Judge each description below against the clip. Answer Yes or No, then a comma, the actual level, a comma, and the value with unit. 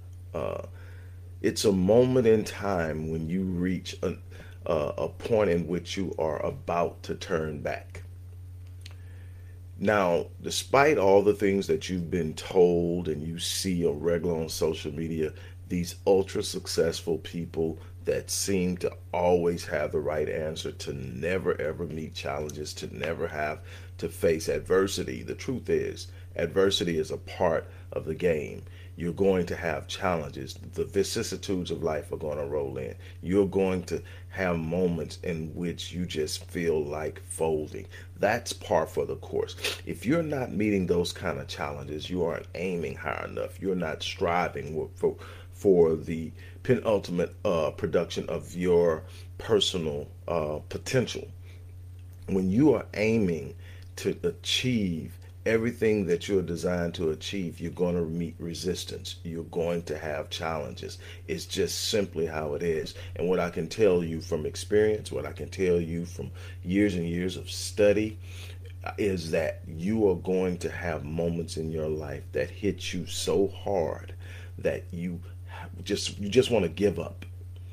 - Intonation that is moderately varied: No, narrow, 1.8 semitones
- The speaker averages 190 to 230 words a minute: No, average, 155 wpm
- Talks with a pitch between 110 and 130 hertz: No, very low, 90 Hz